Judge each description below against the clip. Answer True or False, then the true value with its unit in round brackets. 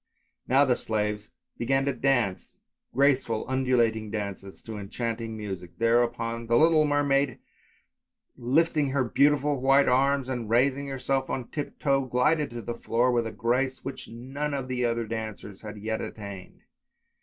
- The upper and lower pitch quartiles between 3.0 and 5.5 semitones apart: True (3.4 semitones)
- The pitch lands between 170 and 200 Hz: False (125 Hz)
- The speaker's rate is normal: True (155 wpm)